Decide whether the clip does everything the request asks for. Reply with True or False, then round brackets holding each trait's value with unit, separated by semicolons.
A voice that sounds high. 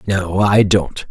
False (95 Hz)